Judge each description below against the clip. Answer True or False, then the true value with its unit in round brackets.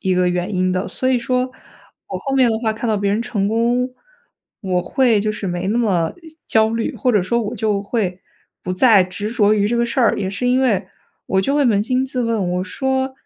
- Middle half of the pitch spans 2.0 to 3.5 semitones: False (4.2 semitones)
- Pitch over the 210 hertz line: True (220 Hz)